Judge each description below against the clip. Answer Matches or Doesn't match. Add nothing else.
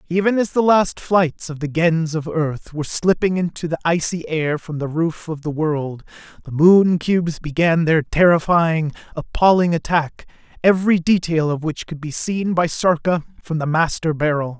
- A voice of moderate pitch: Matches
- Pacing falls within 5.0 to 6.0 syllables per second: Doesn't match